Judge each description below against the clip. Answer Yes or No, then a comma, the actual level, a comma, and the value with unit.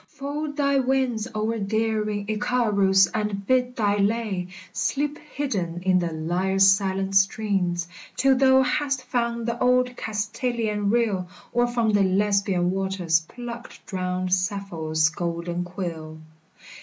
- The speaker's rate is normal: No, slow, 125 wpm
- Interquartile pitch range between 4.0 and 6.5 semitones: Yes, average, 4.6 semitones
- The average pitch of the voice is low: No, high, 205 Hz